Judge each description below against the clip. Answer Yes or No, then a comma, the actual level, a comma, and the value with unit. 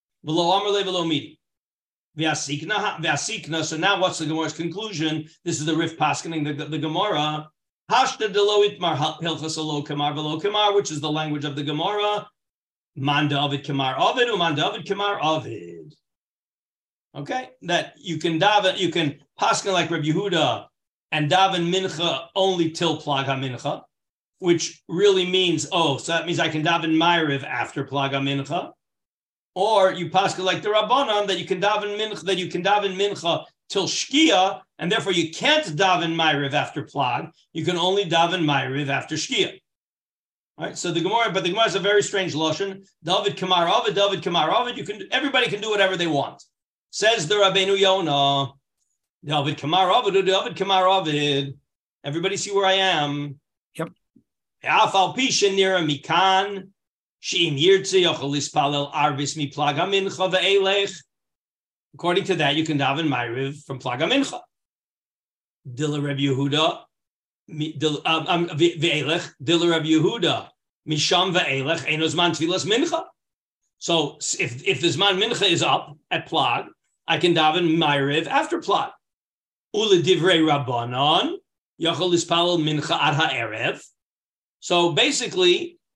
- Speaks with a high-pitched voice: No, medium, 170 Hz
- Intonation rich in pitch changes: No, average, 4.3 semitones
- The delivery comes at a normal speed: No, slow, 120 wpm